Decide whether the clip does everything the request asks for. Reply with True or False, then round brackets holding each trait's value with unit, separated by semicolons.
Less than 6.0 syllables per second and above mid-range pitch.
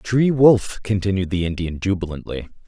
False (4.9 syllables/s; 100 Hz)